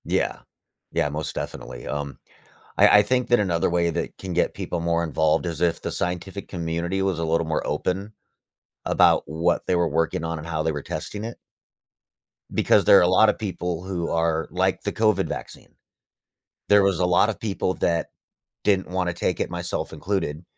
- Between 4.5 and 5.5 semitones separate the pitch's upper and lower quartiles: No, average, 2.7 semitones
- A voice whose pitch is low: Yes, very low, 85 Hz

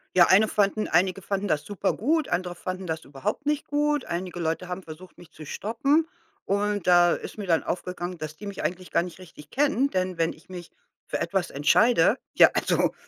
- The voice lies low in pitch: No, medium, 185 Hz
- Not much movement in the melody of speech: No, average, 3.2 semitones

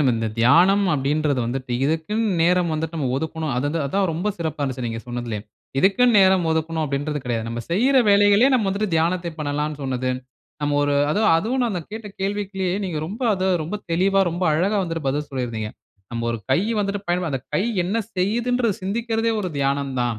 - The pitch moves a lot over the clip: Yes, wide, 6.3 semitones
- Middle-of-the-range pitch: Yes, medium, 165 Hz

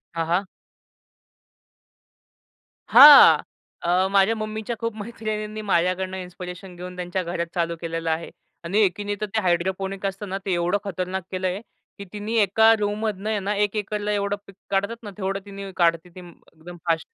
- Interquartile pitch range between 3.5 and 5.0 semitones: No, average, 2.7 semitones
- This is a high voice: Yes, high, 195 Hz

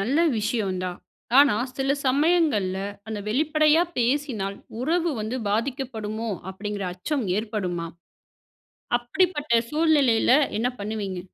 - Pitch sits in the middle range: No, high, 230 Hz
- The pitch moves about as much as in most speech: No, wide, 5.8 semitones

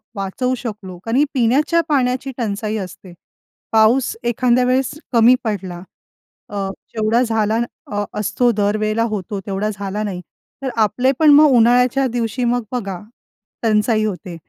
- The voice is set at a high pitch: Yes, high, 225 Hz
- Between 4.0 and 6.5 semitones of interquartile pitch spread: No, average, 3.5 semitones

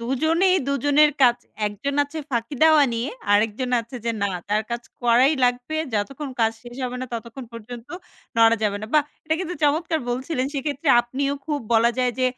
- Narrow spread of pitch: No, average, 3.9 semitones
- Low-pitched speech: No, very high, 255 Hz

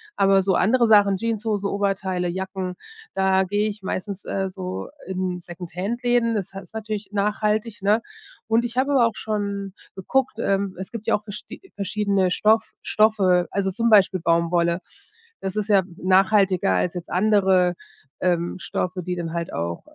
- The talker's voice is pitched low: No, high, 195 Hz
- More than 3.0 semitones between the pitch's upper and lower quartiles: No, narrow, 2.5 semitones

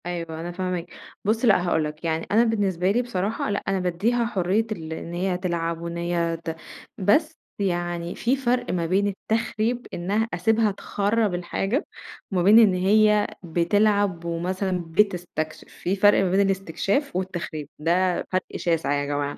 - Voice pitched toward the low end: No, medium, 185 Hz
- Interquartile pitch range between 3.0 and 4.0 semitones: Yes, average, 3.5 semitones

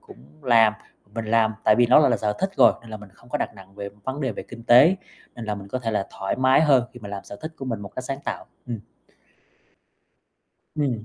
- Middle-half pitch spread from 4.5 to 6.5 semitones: No, average, 3.6 semitones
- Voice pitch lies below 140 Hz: Yes, low, 115 Hz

